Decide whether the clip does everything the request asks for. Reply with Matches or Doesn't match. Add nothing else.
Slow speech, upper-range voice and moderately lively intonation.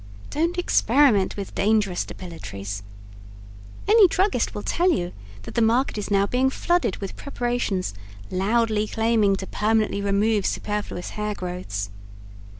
Matches